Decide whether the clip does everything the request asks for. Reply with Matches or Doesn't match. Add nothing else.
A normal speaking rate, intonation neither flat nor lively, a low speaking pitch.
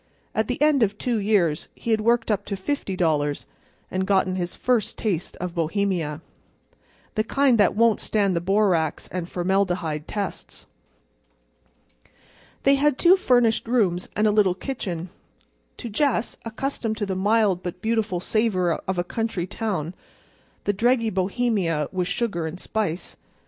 Doesn't match